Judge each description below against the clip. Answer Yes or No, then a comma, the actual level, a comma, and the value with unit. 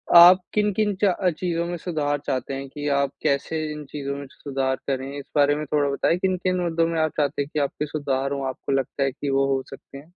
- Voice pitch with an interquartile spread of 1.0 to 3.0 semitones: No, average, 3.4 semitones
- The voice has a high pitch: No, medium, 145 Hz